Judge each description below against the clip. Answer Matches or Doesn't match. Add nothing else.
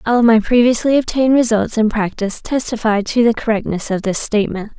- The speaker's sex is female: Matches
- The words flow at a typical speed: Matches